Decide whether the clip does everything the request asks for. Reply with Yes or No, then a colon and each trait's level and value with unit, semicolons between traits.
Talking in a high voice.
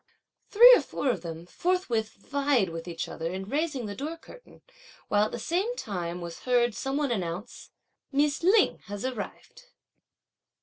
Yes: high, 240 Hz